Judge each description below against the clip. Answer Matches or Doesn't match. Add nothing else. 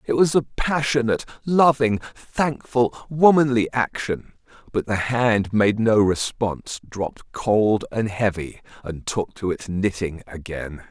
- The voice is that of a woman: Doesn't match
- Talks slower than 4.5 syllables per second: Matches